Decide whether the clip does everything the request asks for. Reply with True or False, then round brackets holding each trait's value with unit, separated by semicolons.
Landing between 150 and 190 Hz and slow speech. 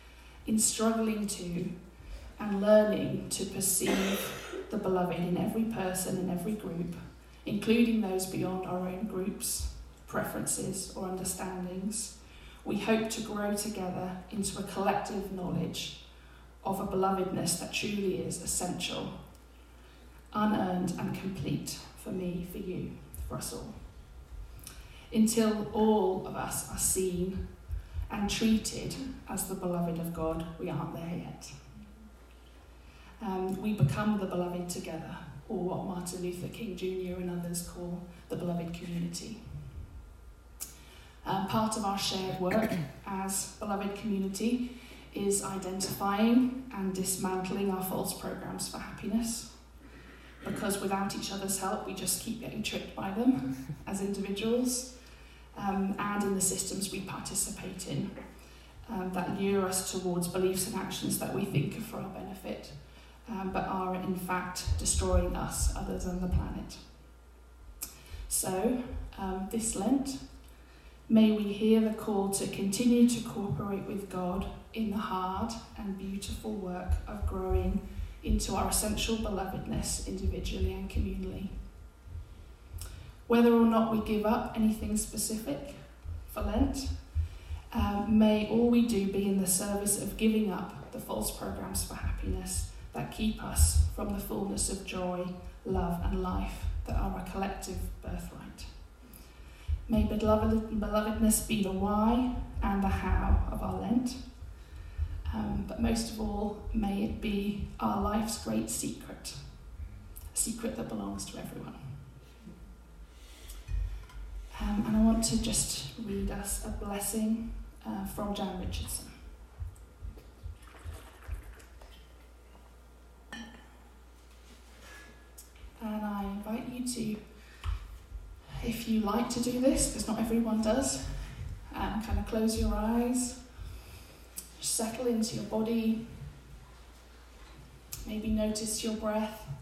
True (185 Hz; 130 wpm)